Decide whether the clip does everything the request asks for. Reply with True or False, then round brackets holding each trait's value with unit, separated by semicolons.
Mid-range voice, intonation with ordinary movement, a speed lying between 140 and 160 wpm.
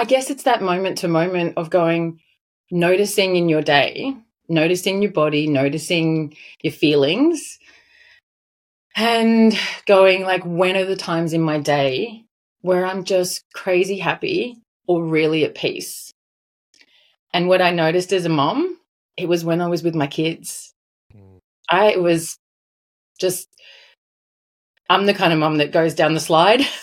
True (180 Hz; 4.0 semitones; 150 wpm)